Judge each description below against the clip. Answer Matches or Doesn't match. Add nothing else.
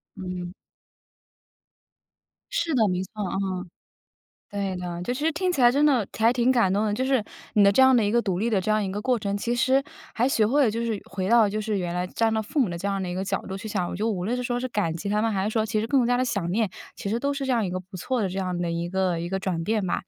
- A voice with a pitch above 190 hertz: Matches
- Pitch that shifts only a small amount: Doesn't match